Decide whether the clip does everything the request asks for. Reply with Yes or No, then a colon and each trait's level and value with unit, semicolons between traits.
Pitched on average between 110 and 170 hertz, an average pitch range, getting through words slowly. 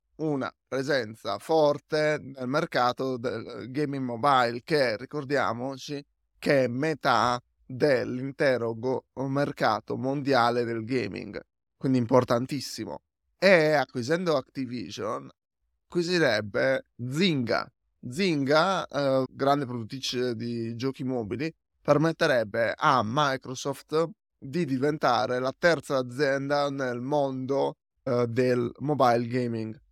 Yes: low, 135 Hz; average, 3.0 semitones; slow, 95 wpm